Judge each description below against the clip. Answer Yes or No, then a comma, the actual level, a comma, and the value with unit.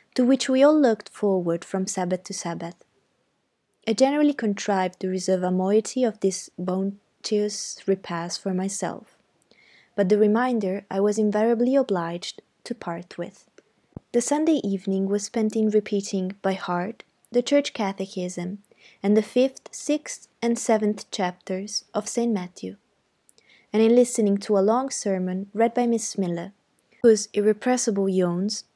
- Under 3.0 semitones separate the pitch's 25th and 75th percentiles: No, average, 3.5 semitones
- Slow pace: No, average, 145 wpm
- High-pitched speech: Yes, high, 205 Hz